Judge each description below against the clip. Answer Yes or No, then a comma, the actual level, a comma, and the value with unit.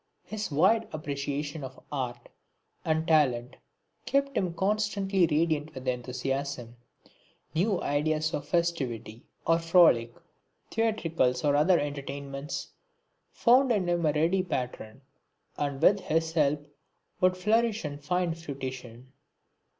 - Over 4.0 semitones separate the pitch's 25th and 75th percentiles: Yes, average, 4.7 semitones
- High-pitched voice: No, medium, 155 Hz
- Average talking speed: No, slow, 115 wpm